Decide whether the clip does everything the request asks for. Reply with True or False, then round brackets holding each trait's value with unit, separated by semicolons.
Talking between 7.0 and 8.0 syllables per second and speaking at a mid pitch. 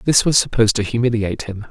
False (7.1 syllables/s; 115 Hz)